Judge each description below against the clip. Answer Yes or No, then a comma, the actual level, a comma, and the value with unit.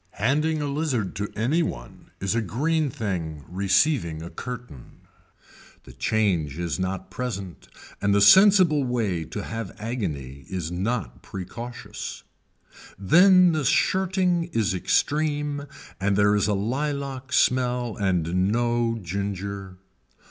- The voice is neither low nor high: No, low, 110 Hz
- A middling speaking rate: No, slow, 125 wpm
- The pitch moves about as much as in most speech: No, wide, 6.8 semitones